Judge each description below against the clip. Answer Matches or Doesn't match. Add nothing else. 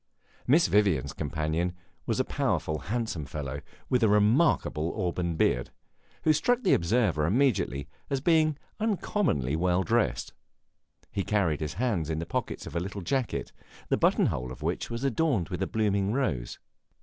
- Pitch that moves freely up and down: Matches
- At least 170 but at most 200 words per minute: Doesn't match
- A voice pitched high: Doesn't match